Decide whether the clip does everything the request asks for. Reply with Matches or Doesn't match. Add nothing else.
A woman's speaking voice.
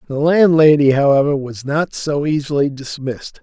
Doesn't match